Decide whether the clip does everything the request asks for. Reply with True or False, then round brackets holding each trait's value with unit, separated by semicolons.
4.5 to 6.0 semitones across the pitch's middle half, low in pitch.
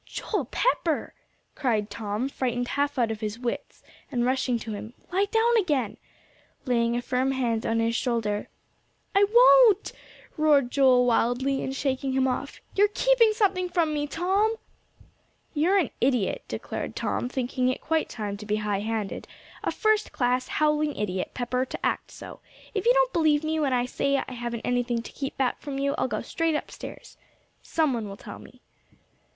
False (5.1 semitones; 265 Hz)